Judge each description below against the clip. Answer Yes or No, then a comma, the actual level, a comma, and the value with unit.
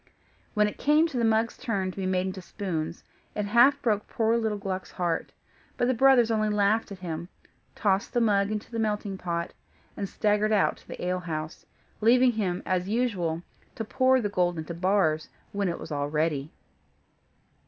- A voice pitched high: Yes, high, 200 Hz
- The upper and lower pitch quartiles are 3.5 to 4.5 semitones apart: Yes, average, 4.0 semitones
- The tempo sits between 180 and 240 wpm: Yes, average, 185 wpm